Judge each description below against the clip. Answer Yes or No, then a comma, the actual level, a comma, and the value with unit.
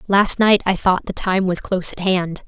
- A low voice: No, high, 190 Hz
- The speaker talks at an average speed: No, fast, 245 wpm